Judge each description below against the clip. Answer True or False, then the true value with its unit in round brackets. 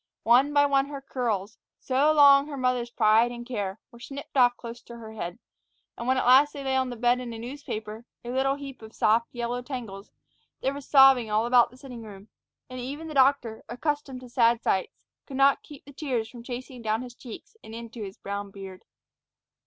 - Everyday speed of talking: False (215 wpm)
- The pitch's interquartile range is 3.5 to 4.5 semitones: False (3.1 semitones)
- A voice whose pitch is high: True (245 Hz)